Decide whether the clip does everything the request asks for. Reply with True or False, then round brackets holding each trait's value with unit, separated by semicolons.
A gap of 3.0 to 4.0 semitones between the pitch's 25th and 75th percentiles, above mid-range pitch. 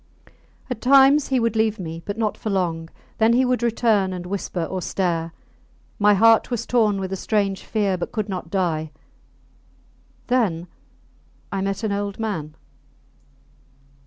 True (3.6 semitones; 200 Hz)